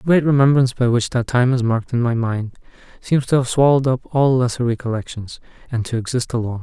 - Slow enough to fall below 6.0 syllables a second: No, 6.4 syllables/s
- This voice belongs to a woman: No, male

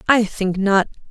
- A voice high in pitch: Yes, high, 205 Hz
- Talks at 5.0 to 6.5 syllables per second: No, 4.1 syllables/s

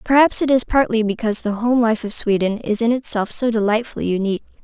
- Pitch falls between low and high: No, high, 225 Hz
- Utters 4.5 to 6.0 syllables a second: No, 6.2 syllables/s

